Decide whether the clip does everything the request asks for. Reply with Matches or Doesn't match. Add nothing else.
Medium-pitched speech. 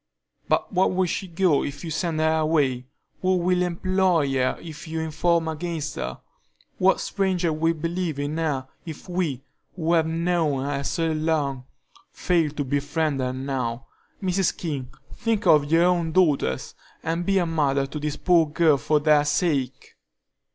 Matches